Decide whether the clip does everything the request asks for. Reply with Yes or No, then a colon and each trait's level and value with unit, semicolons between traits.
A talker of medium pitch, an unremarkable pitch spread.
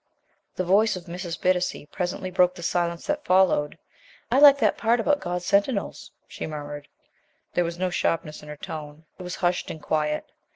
Yes: medium, 175 Hz; average, 3.2 semitones